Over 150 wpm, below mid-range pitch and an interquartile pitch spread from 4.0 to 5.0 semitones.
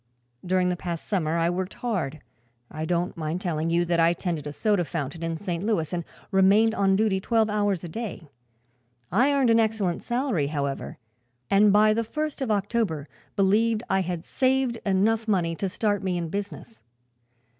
No: average, 175 wpm; high, 190 Hz; average, 4.5 semitones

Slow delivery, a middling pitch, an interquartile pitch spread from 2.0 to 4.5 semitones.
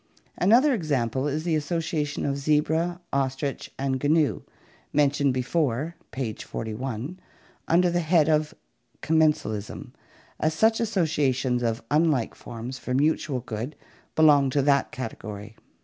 Yes: slow, 120 wpm; medium, 145 Hz; average, 3.7 semitones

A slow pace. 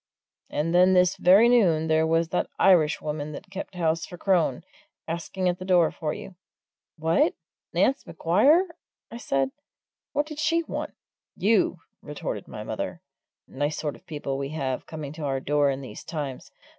No: average, 165 wpm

